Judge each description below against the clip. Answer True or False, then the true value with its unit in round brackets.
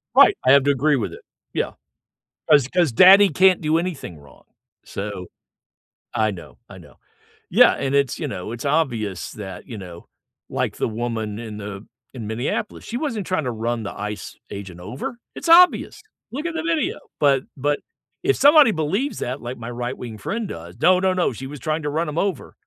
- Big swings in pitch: True (8.9 semitones)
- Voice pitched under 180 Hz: True (135 Hz)